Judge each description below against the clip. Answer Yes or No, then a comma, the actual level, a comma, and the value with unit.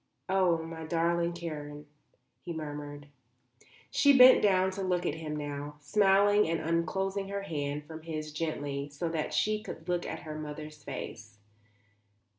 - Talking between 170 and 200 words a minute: No, average, 150 wpm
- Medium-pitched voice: Yes, medium, 160 Hz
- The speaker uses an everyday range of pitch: Yes, average, 3.9 semitones